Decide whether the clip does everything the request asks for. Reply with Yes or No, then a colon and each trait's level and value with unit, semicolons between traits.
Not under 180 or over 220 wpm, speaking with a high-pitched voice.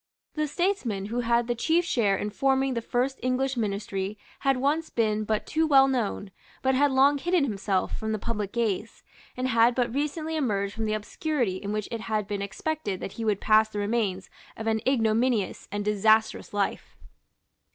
Yes: average, 185 wpm; high, 230 Hz